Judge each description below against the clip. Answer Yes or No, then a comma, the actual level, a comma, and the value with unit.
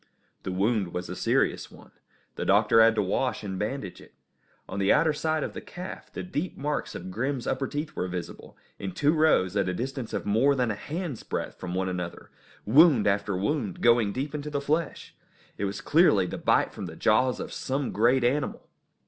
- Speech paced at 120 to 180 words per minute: No, fast, 205 wpm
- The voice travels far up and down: Yes, wide, 6.7 semitones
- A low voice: Yes, low, 120 Hz